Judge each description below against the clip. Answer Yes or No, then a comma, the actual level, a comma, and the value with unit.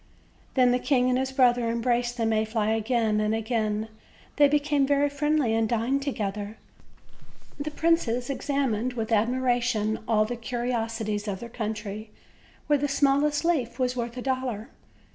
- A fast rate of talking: No, average, 155 wpm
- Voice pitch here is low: No, high, 240 Hz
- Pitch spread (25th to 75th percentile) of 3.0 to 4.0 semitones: Yes, average, 3.4 semitones